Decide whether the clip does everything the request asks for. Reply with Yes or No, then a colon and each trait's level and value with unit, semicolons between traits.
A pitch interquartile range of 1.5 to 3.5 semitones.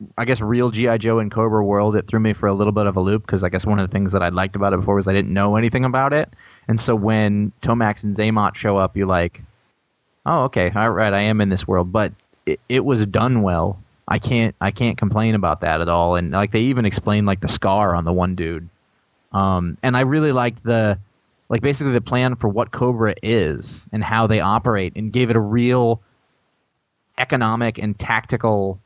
Yes: average, 2.9 semitones